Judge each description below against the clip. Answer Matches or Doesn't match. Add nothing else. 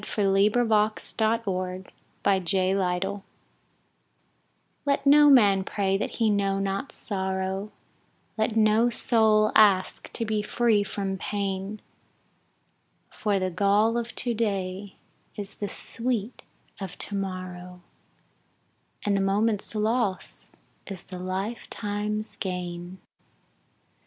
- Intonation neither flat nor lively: Doesn't match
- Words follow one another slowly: Matches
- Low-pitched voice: Doesn't match